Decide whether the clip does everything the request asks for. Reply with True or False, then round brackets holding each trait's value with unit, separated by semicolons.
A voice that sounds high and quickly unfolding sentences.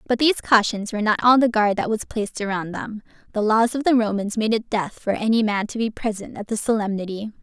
True (215 Hz; 240 wpm)